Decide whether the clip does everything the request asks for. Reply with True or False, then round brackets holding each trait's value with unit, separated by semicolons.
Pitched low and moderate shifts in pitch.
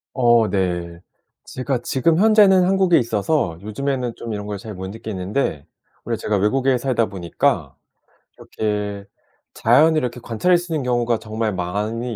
True (115 Hz; 4.8 semitones)